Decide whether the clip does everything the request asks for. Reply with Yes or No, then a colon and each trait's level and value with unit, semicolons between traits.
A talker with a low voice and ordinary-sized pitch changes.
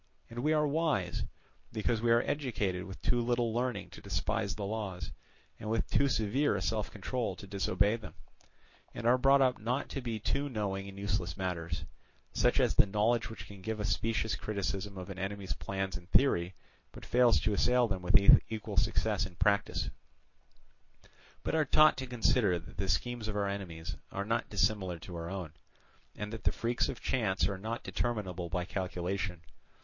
Yes: low, 105 Hz; average, 3.8 semitones